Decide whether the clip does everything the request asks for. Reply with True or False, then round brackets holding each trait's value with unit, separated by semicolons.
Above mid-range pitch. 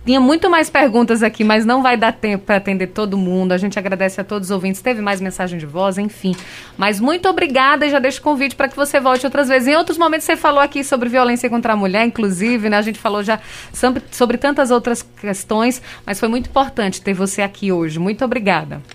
True (230 Hz)